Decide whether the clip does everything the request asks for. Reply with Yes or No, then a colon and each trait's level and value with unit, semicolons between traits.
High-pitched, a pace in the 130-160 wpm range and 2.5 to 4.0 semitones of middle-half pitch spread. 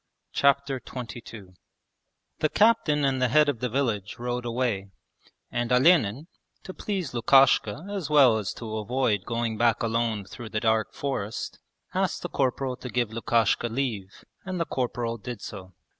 No: low, 120 Hz; average, 155 wpm; average, 3.7 semitones